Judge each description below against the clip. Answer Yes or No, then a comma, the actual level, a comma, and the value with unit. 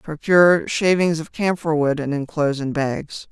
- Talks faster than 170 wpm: No, average, 165 wpm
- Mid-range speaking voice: Yes, medium, 155 Hz